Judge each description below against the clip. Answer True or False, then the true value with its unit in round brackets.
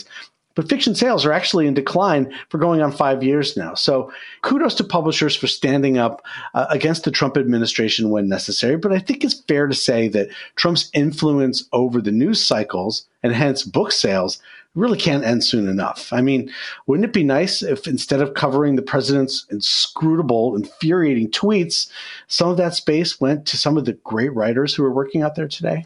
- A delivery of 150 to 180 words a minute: False (190 wpm)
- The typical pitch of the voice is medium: True (145 Hz)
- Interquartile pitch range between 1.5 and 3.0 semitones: False (4.4 semitones)